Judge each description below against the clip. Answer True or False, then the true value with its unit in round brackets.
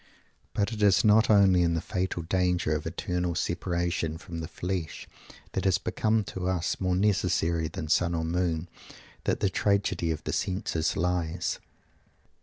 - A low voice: True (90 Hz)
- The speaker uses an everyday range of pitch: False (2.3 semitones)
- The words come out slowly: False (160 wpm)